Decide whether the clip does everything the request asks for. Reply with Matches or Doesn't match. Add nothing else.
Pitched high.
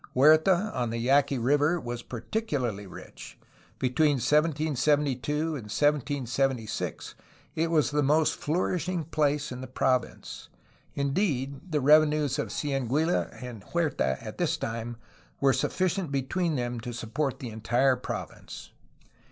Doesn't match